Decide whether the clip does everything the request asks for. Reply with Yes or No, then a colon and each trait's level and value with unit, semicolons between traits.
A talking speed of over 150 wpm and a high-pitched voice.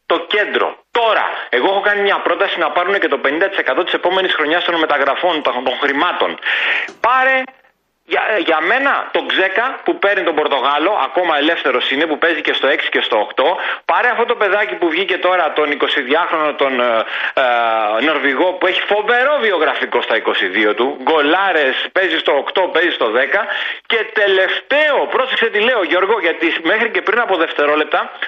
Yes: fast, 170 wpm; high, 195 Hz